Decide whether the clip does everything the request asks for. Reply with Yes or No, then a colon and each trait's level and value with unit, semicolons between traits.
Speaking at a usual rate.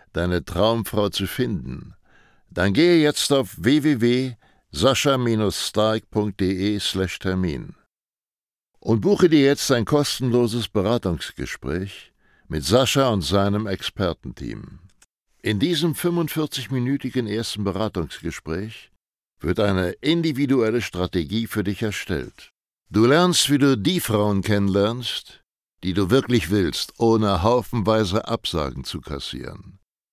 No: slow, 100 wpm